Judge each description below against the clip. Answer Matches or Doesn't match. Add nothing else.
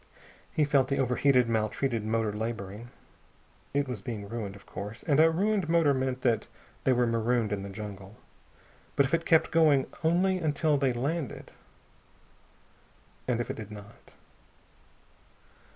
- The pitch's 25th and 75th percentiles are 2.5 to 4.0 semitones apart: Doesn't match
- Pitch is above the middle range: Doesn't match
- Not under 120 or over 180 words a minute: Matches